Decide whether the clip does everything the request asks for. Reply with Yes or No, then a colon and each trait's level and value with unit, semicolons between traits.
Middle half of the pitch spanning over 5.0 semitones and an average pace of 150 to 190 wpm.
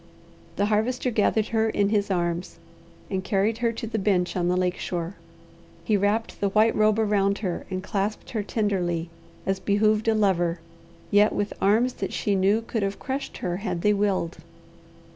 No: narrow, 2.6 semitones; average, 180 wpm